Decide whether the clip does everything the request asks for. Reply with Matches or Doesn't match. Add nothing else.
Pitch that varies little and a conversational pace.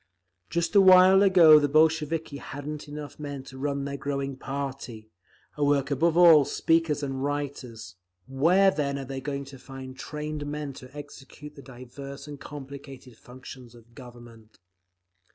Matches